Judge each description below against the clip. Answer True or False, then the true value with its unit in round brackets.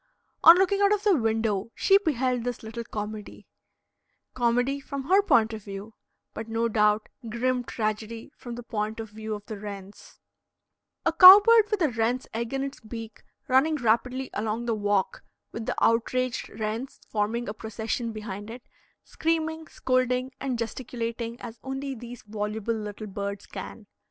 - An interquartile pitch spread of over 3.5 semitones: False (3.2 semitones)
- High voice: True (230 Hz)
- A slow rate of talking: False (160 wpm)